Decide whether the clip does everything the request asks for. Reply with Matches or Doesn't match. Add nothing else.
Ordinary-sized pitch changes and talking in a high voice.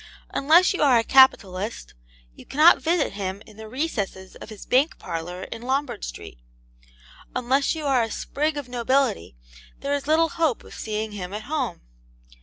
Doesn't match